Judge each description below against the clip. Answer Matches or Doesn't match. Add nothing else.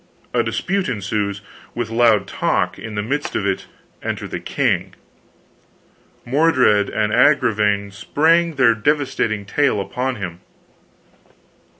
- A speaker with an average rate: Doesn't match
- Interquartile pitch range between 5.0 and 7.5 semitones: Matches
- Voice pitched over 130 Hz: Doesn't match